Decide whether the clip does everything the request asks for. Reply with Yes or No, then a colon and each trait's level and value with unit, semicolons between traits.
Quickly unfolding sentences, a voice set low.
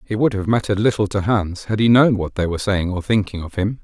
Yes: fast, 280 wpm; low, 105 Hz